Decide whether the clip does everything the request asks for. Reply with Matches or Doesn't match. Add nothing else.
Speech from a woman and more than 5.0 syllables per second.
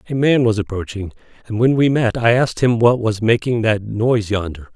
Doesn't match